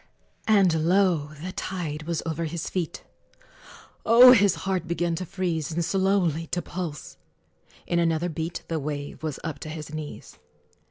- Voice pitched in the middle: Yes, medium, 170 Hz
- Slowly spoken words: No, average, 155 wpm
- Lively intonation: No, average, 2.8 semitones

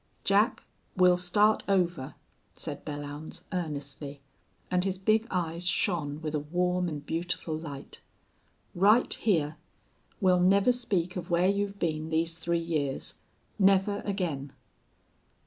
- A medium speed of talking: No, slow, 125 wpm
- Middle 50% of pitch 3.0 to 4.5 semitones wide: Yes, average, 3.7 semitones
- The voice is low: No, medium, 175 Hz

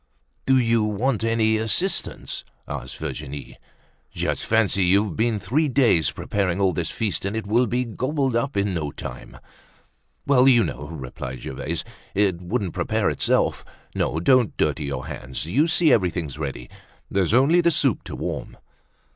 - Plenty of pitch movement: Yes, wide, 6.9 semitones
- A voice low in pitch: Yes, low, 105 Hz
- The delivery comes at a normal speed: Yes, average, 155 wpm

